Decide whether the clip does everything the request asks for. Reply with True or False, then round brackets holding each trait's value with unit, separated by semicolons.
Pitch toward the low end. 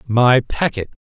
True (125 Hz)